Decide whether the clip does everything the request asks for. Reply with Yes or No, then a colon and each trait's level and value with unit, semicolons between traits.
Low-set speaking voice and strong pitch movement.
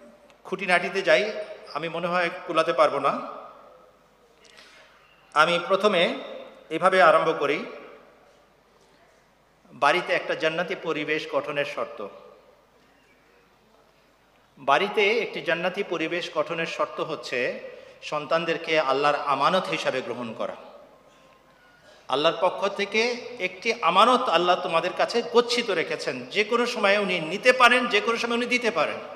No: medium, 185 Hz; wide, 6.0 semitones